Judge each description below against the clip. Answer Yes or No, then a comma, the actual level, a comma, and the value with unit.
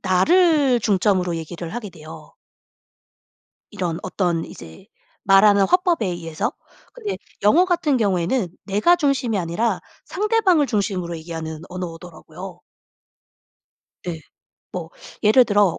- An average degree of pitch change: No, wide, 7.5 semitones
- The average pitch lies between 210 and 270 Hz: No, high, 195 Hz